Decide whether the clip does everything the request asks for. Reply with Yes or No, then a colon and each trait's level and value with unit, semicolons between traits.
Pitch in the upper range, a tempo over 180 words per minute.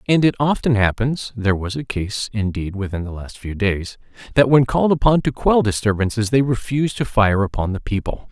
No: low, 115 Hz; average, 200 wpm